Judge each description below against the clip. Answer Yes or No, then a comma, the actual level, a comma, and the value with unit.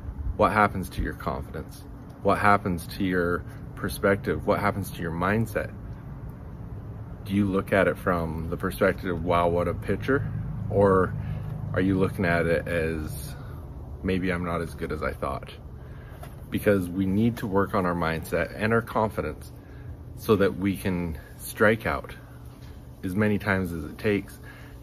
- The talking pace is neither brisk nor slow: Yes, average, 160 wpm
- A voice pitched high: No, low, 100 Hz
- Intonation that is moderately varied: Yes, average, 3.4 semitones